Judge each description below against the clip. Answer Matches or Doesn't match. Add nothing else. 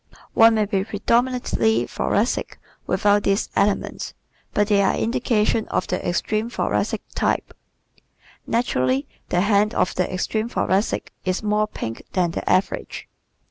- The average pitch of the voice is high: Matches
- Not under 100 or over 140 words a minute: Matches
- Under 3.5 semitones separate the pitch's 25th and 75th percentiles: Matches